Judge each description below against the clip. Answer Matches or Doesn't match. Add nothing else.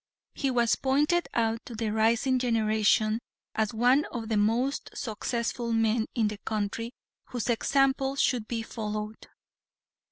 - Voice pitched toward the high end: Matches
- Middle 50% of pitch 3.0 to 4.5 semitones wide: Doesn't match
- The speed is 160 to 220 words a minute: Doesn't match